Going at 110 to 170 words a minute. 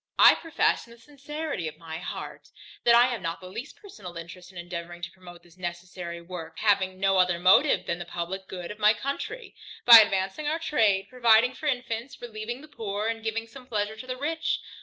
No: fast, 205 wpm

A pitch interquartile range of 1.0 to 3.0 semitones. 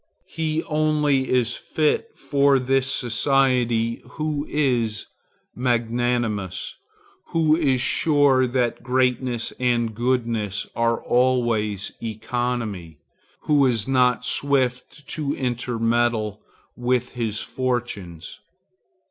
Yes: average, 2.7 semitones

